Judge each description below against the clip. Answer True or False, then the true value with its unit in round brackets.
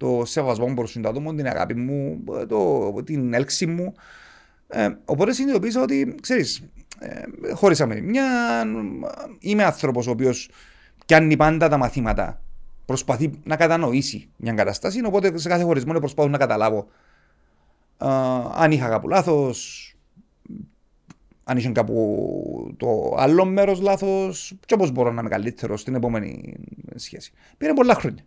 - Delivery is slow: False (135 wpm)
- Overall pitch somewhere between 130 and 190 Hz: True (140 Hz)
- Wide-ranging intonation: True (7.8 semitones)